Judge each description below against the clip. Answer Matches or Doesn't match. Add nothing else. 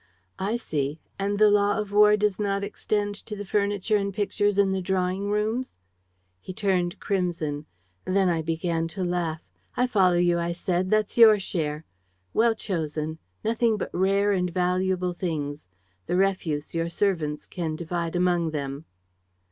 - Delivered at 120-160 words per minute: Matches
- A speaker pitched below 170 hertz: Doesn't match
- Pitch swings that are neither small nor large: Matches